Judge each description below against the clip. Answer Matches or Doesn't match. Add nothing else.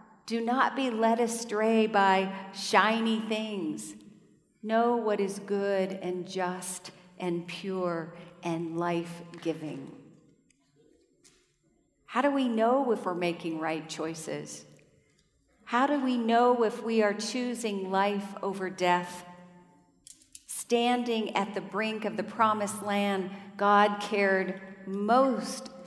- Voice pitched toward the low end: Doesn't match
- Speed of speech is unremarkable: Doesn't match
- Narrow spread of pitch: Doesn't match